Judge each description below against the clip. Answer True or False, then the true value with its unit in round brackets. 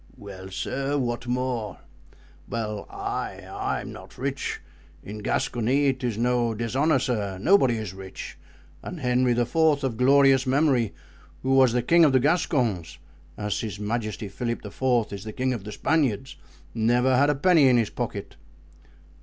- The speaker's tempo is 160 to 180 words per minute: False (145 wpm)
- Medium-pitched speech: False (120 Hz)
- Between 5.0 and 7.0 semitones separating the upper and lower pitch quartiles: False (3.8 semitones)